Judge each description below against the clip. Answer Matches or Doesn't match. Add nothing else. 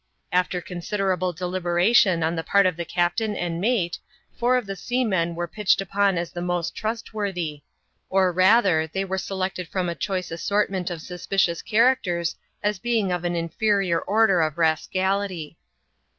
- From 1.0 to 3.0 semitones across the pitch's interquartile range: Matches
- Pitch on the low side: Doesn't match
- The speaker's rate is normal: Matches